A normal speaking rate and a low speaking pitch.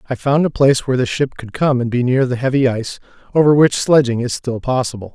No: fast, 245 wpm; low, 130 Hz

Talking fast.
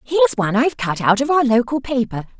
Yes: fast, 250 wpm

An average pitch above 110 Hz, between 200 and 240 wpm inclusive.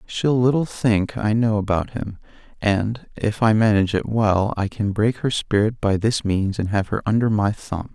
No: low, 105 Hz; fast, 205 wpm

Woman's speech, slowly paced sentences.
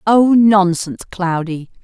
Yes: female; slow, 100 wpm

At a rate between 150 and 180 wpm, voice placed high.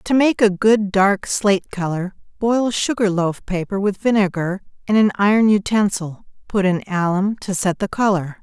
Yes: average, 165 wpm; high, 200 Hz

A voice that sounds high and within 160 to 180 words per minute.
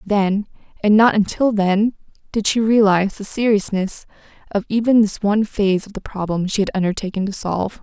Yes: high, 205 Hz; average, 175 wpm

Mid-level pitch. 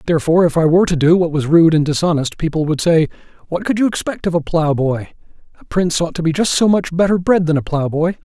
Yes: medium, 165 Hz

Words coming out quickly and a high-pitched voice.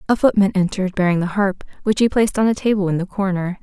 Yes: fast, 250 wpm; high, 195 Hz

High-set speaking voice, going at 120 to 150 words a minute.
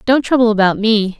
No: high, 220 Hz; average, 200 wpm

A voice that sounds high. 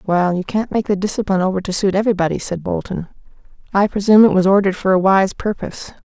Yes: high, 195 Hz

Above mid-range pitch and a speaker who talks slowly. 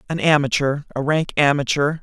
No: medium, 145 Hz; slow, 120 wpm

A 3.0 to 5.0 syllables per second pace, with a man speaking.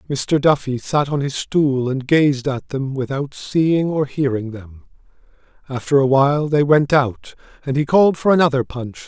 Yes: 4.5 syllables/s; male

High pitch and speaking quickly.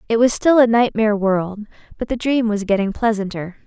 No: high, 220 Hz; average, 195 wpm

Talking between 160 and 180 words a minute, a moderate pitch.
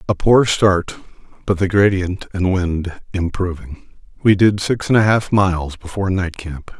No: average, 170 wpm; very low, 95 Hz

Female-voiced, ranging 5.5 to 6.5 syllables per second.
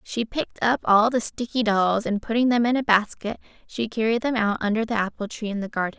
Yes: female; 5.8 syllables/s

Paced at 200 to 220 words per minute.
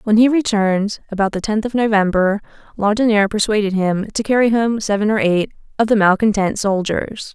No: average, 170 wpm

